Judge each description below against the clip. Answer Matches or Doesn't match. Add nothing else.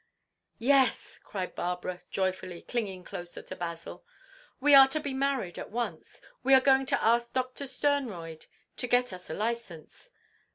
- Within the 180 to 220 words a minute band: Doesn't match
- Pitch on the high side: Matches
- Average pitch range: Doesn't match